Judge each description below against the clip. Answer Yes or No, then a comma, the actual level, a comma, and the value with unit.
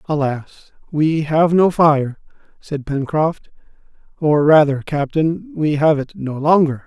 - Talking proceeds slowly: Yes, slow, 130 wpm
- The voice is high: No, medium, 150 Hz